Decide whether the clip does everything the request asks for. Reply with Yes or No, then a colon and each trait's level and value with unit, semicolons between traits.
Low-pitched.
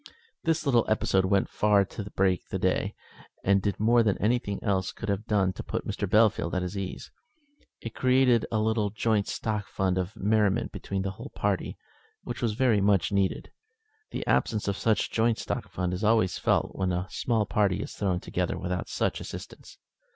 Yes: low, 100 Hz